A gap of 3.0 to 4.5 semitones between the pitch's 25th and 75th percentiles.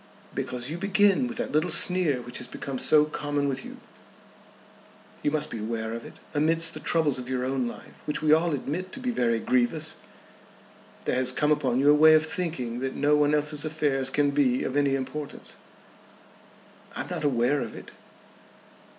Yes: average, 3.4 semitones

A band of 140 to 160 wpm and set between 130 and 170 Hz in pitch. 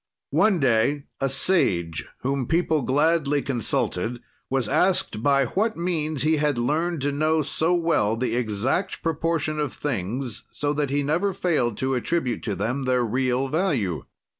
Yes: average, 155 wpm; medium, 140 Hz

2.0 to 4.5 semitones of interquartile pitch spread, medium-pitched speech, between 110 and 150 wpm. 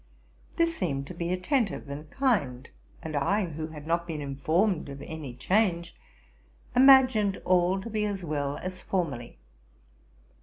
No: wide, 5.5 semitones; medium, 170 Hz; average, 145 wpm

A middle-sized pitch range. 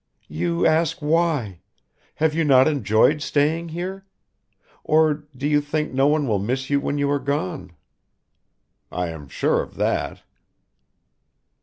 Yes: average, 4.2 semitones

